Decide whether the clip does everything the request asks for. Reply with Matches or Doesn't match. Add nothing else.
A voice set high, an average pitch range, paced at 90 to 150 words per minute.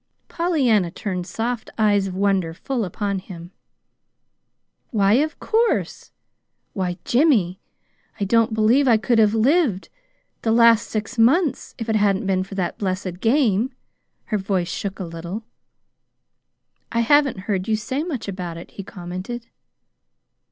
Matches